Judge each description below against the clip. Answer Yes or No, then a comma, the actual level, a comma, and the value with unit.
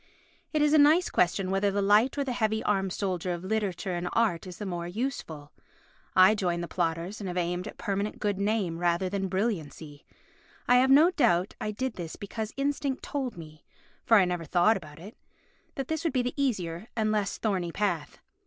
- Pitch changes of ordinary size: Yes, average, 4.7 semitones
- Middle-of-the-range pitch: No, high, 200 Hz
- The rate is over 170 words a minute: Yes, average, 200 wpm